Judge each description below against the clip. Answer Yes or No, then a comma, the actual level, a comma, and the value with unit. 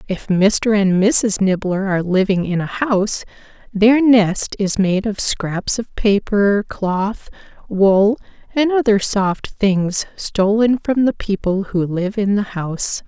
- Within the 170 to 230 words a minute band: No, average, 150 wpm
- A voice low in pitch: No, high, 205 Hz